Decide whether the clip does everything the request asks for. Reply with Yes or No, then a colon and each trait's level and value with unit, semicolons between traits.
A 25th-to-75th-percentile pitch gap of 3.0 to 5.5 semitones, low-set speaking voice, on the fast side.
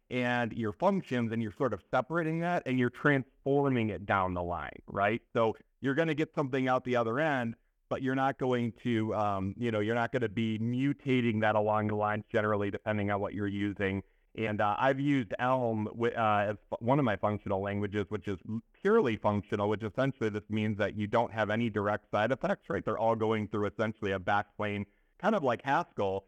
Yes: average, 3.6 semitones; low, 110 Hz; fast, 210 wpm